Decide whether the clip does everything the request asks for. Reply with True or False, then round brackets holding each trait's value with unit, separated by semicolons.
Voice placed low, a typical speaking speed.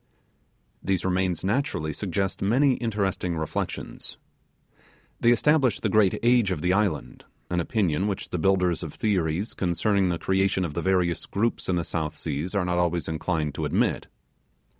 True (95 Hz; 160 wpm)